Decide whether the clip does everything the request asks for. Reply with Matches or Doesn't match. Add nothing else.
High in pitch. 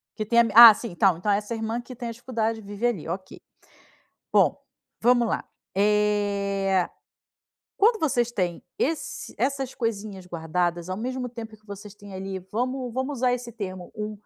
Matches